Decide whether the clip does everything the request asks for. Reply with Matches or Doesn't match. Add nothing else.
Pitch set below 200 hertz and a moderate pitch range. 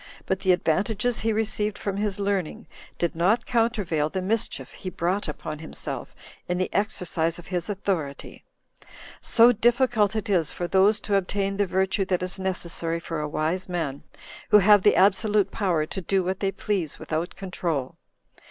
Matches